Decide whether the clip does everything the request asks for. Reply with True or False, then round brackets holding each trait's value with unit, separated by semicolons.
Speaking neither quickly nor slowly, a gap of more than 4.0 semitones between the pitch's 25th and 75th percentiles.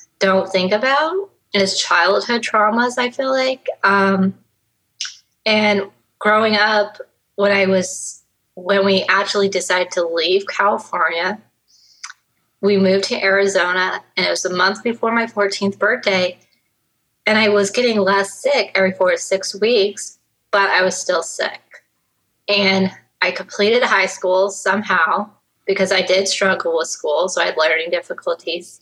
False (145 wpm; 3.4 semitones)